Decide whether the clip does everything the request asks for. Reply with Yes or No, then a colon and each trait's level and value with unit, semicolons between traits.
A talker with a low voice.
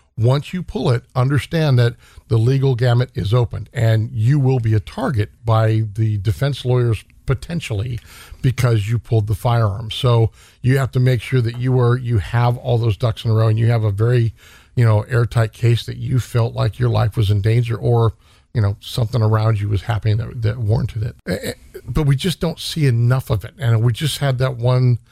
Yes: low, 120 Hz